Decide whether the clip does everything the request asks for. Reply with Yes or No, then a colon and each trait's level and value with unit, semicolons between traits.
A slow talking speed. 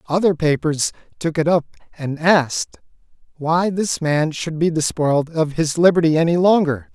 No: average, 155 wpm